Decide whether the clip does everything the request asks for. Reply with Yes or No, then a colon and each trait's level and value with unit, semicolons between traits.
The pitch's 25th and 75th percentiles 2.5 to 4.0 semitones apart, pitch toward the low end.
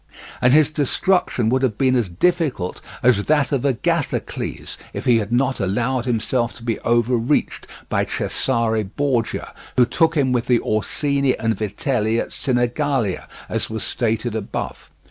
Yes: average, 3.4 semitones; low, 120 Hz